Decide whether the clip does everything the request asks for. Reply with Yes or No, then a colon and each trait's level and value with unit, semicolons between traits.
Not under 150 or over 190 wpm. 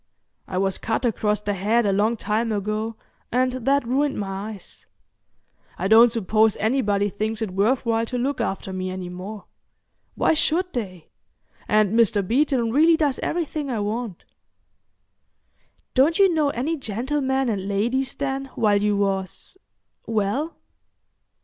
No: average, 140 wpm